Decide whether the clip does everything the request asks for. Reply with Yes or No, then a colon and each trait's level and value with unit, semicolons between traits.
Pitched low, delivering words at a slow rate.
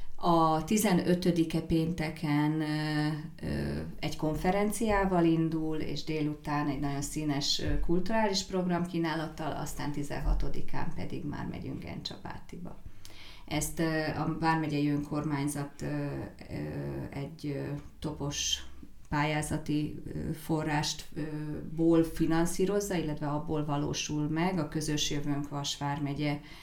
No: medium, 150 Hz; slow, 85 wpm